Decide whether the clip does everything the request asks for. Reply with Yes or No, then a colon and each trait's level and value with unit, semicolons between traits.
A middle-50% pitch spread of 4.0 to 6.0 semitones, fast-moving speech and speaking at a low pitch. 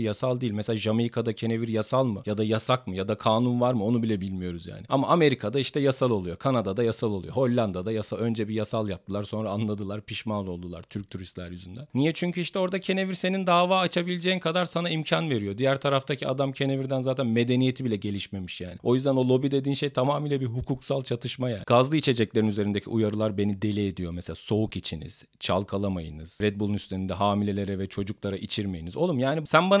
Yes: average, 5.0 semitones; fast, 190 wpm; low, 115 Hz